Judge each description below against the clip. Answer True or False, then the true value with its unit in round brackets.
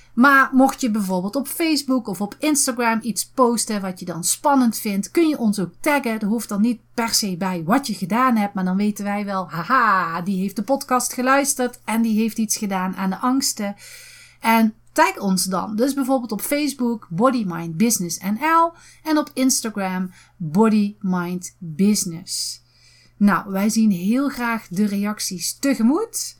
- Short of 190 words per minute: True (165 wpm)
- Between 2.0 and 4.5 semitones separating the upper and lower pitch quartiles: False (5.3 semitones)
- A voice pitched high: True (220 Hz)